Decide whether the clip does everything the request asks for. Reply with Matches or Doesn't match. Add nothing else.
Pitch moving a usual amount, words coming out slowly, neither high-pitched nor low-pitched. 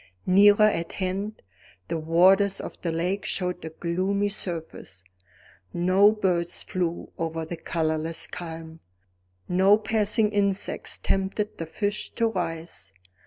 Matches